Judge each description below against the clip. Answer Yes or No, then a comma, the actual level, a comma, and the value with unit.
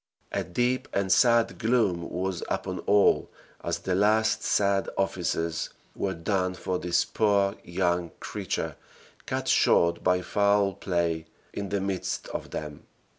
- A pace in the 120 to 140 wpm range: Yes, slow, 135 wpm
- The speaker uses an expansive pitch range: No, average, 2.7 semitones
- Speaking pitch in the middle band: No, very low, 95 Hz